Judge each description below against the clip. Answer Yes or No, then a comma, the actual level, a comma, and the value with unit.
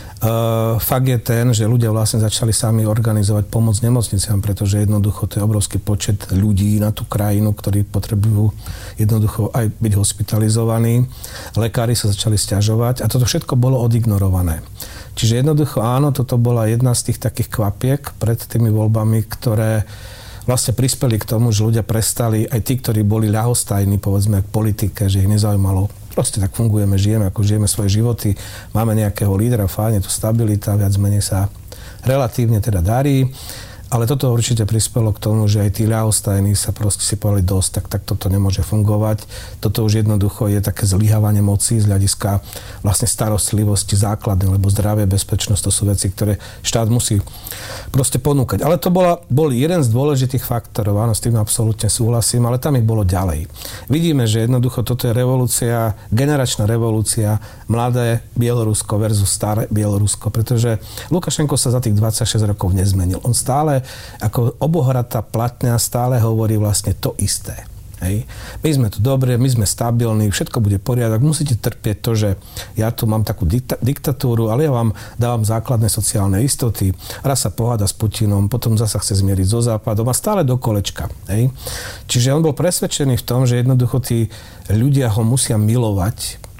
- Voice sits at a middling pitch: No, low, 110 Hz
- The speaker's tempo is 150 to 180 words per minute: Yes, fast, 165 wpm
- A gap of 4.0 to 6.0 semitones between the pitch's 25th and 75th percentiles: No, average, 2.7 semitones